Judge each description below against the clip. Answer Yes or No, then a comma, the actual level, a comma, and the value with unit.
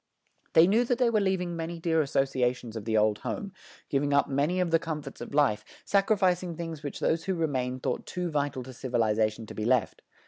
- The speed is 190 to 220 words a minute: Yes, fast, 205 wpm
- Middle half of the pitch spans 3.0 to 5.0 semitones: No, wide, 5.6 semitones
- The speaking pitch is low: No, medium, 150 Hz